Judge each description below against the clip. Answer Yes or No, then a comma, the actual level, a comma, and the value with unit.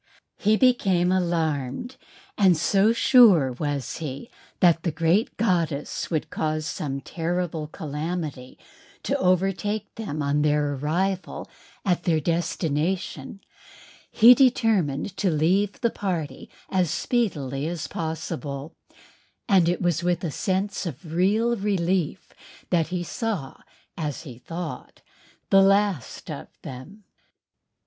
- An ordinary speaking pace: No, slow, 120 wpm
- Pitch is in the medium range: Yes, medium, 175 Hz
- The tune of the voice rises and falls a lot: No, average, 4.3 semitones